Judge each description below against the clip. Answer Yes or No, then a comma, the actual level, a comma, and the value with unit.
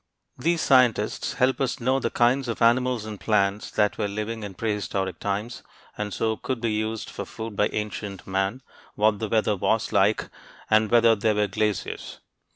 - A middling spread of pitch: No, narrow, 2.2 semitones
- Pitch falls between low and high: No, low, 110 Hz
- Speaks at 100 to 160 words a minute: No, average, 180 wpm